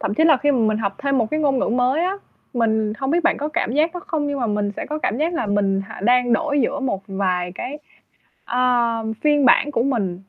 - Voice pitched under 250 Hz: No, very high, 255 Hz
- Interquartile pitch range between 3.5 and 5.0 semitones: No, wide, 5.6 semitones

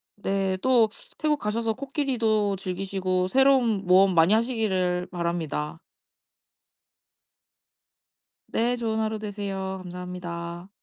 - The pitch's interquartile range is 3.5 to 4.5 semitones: Yes, average, 3.8 semitones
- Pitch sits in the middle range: No, high, 195 Hz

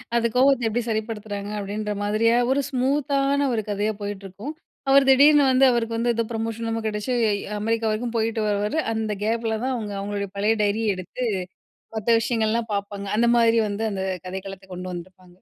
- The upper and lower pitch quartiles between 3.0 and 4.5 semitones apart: No, narrow, 2.6 semitones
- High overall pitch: Yes, high, 220 Hz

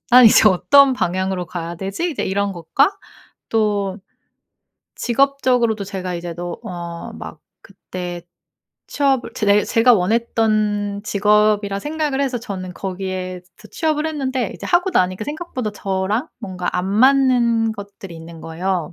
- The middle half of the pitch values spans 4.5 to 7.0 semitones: Yes, average, 5.2 semitones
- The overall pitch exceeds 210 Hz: No, high, 205 Hz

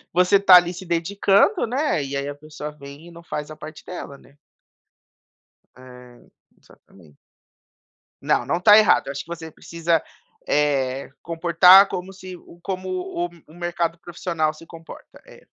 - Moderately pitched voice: Yes, medium, 170 Hz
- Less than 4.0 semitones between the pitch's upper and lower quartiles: Yes, average, 3.6 semitones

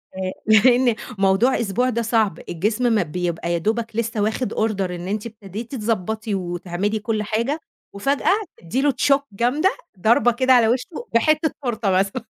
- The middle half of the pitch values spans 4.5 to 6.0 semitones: No, average, 3.8 semitones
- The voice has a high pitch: Yes, high, 220 Hz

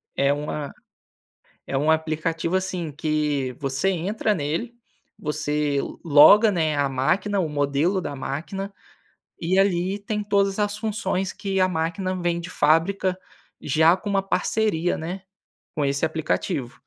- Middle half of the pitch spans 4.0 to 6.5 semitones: Yes, average, 4.5 semitones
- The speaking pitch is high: No, medium, 165 Hz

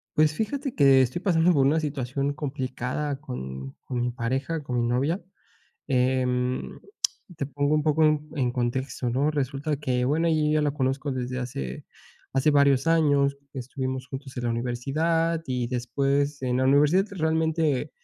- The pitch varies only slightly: No, average, 3.2 semitones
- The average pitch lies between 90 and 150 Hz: Yes, medium, 140 Hz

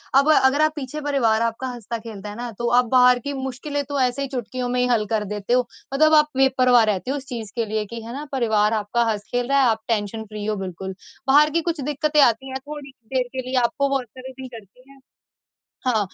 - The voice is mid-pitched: No, very high, 250 Hz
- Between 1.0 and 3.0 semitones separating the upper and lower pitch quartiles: No, average, 3.6 semitones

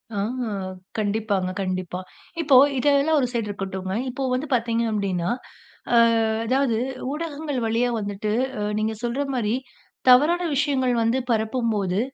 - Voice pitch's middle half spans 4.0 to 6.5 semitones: Yes, average, 4.8 semitones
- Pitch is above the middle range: Yes, high, 230 Hz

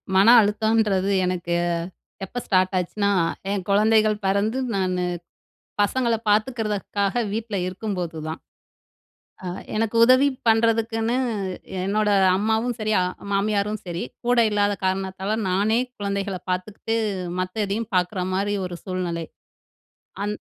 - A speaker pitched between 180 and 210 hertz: Yes, high, 205 Hz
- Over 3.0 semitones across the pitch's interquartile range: No, average, 2.7 semitones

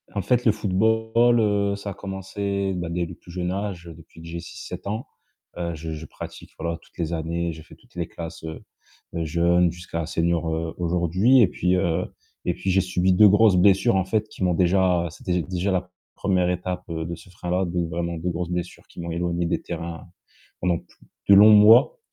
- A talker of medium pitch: No, very low, 90 Hz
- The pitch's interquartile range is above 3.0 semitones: No, narrow, 2.6 semitones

